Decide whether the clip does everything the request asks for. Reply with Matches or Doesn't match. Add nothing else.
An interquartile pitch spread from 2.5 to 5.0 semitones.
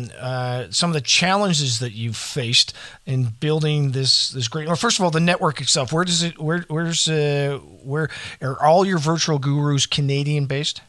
Matches